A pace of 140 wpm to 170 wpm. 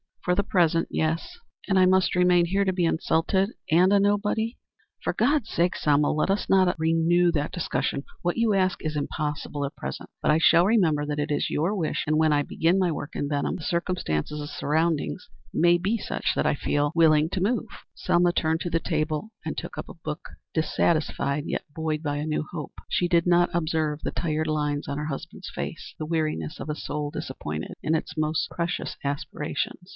No: fast, 205 wpm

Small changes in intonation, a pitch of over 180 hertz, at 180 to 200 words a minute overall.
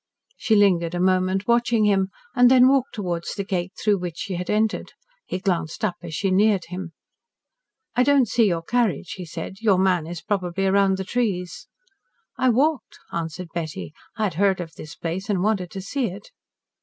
No: average, 3.5 semitones; high, 190 Hz; average, 190 wpm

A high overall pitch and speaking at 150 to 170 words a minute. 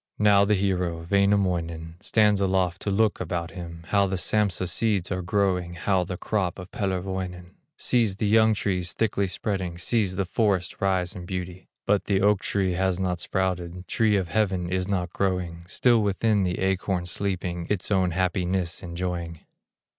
No: very low, 95 Hz; average, 165 wpm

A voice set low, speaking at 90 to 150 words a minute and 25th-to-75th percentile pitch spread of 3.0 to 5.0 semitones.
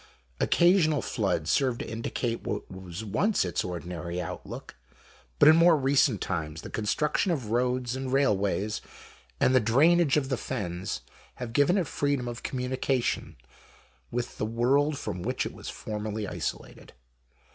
No: low, 120 Hz; average, 145 wpm; wide, 5.4 semitones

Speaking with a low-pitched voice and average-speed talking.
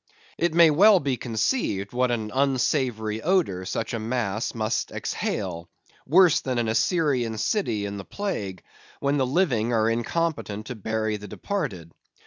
Yes: low, 120 Hz; average, 150 wpm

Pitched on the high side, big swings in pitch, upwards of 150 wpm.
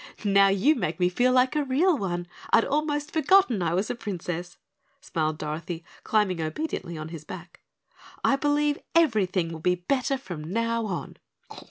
Yes: high, 200 Hz; wide, 7.9 semitones; average, 165 wpm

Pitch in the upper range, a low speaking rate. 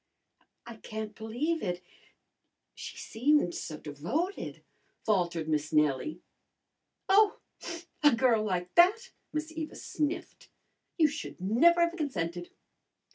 Yes: high, 230 Hz; slow, 110 wpm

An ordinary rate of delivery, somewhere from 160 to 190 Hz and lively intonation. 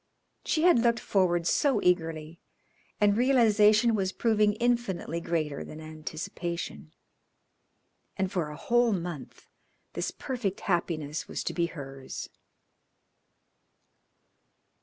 No: slow, 105 wpm; medium, 185 Hz; wide, 5.8 semitones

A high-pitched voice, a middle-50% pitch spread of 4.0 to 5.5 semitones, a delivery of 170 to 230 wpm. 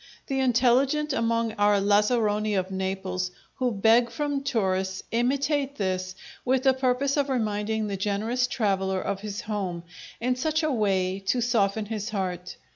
No: high, 220 Hz; average, 4.6 semitones; average, 150 wpm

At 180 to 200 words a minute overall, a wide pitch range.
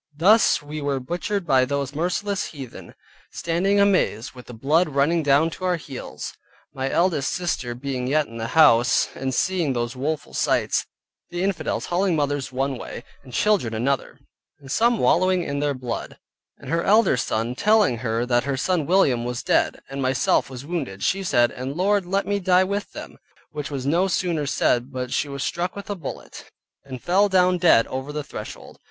Yes: average, 185 wpm; wide, 5.8 semitones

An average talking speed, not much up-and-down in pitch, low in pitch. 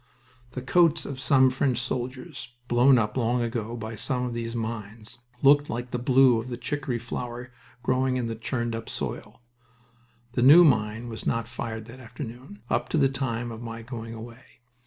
Yes: average, 180 wpm; narrow, 2.0 semitones; low, 120 Hz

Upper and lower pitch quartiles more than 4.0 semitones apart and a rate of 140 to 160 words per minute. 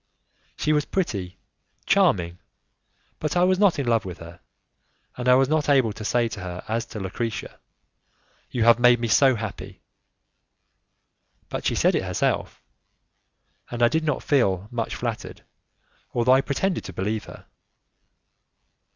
Yes: average, 5.2 semitones; average, 150 wpm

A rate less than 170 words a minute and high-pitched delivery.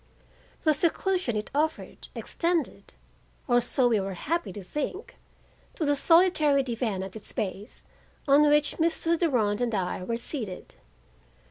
Yes: average, 140 wpm; very high, 275 Hz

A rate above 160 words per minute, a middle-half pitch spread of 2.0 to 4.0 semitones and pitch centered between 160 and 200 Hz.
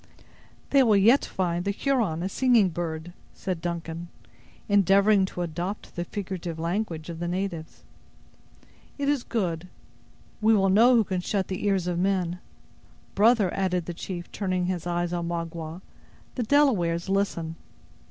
No: average, 150 wpm; average, 2.9 semitones; medium, 185 Hz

